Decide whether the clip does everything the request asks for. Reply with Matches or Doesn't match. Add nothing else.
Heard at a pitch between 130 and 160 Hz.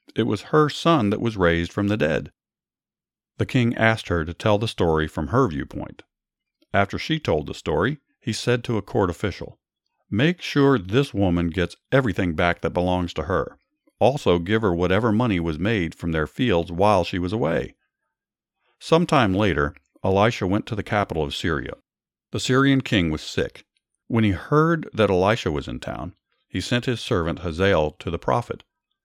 Doesn't match